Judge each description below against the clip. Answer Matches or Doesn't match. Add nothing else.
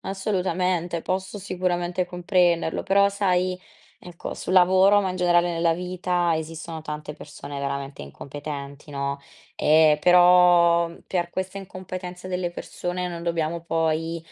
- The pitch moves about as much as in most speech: Doesn't match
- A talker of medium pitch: Matches